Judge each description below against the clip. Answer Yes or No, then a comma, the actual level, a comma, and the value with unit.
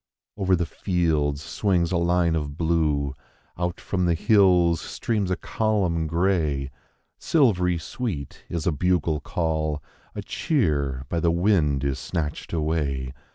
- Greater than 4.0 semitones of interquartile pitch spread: No, average, 3.5 semitones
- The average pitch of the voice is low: Yes, very low, 85 Hz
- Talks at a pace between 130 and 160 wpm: Yes, average, 150 wpm